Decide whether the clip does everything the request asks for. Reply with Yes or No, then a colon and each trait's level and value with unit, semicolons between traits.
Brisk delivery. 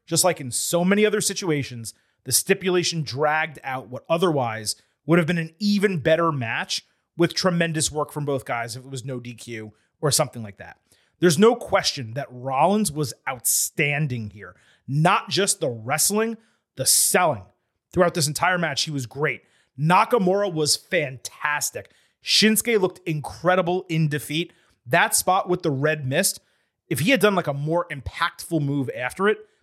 No: average, 165 wpm